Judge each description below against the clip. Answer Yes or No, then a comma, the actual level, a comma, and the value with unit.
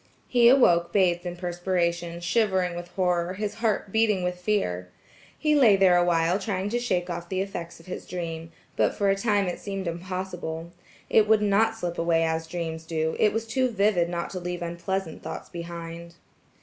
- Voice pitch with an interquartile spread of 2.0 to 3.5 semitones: Yes, average, 2.9 semitones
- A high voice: No, medium, 180 Hz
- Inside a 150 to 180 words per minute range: No, average, 190 wpm